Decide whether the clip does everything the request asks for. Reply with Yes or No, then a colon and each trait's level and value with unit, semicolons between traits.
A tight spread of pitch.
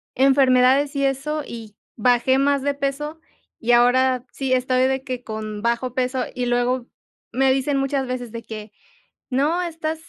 Yes: narrow, 2.1 semitones